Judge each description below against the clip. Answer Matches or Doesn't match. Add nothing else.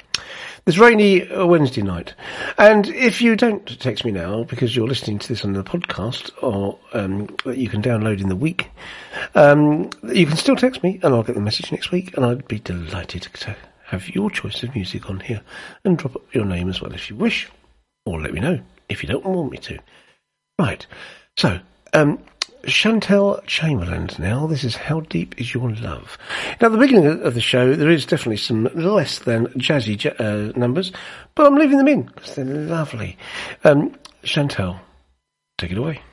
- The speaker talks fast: Doesn't match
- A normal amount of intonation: Doesn't match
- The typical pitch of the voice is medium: Doesn't match